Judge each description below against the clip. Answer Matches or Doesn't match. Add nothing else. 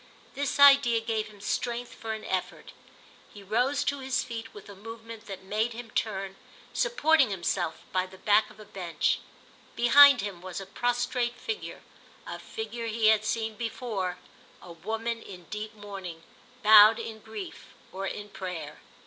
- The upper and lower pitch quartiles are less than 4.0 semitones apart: Matches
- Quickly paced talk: Doesn't match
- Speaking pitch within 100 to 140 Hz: Doesn't match